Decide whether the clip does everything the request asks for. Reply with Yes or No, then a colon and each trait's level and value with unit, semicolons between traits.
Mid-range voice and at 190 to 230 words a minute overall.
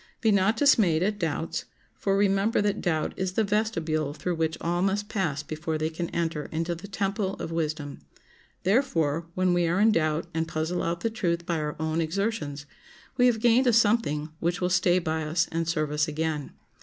Yes: medium, 170 Hz; average, 195 wpm